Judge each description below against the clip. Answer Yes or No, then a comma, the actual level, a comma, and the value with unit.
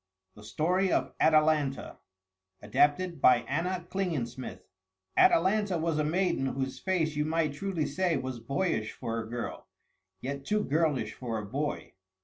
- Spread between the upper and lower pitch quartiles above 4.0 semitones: Yes, average, 5.2 semitones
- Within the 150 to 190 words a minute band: No, average, 140 wpm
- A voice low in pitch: No, medium, 150 Hz